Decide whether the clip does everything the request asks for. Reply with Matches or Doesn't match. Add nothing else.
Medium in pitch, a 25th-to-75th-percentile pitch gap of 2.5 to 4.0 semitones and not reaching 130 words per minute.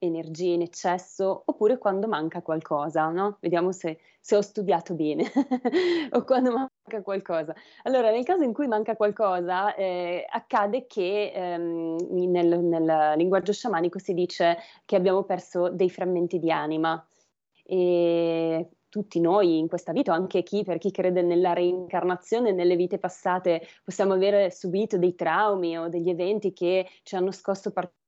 Doesn't match